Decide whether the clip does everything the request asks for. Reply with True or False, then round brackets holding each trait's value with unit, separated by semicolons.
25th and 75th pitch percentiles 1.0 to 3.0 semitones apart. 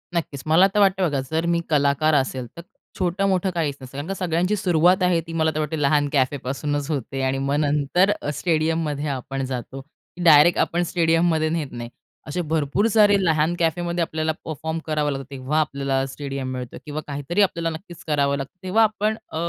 False (3.6 semitones)